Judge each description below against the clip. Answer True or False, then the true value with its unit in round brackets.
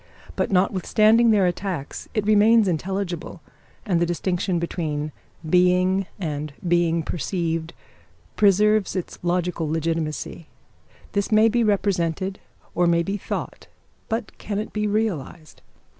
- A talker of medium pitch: True (180 Hz)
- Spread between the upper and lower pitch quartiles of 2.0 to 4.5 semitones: True (3.5 semitones)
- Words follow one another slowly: True (120 wpm)